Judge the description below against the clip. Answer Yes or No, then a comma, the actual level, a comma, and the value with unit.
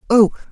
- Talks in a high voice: Yes, high, 220 Hz